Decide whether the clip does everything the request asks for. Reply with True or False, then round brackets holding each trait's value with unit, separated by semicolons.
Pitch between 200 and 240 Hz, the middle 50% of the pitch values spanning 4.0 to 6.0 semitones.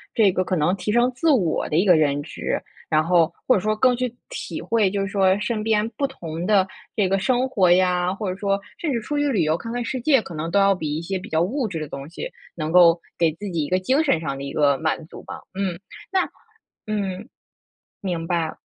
False (190 Hz; 5.0 semitones)